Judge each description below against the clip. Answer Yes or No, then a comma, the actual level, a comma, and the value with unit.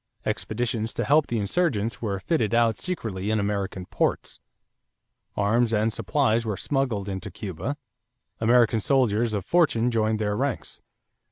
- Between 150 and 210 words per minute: No, average, 140 wpm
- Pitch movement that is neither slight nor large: Yes, average, 3.0 semitones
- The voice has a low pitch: Yes, low, 110 Hz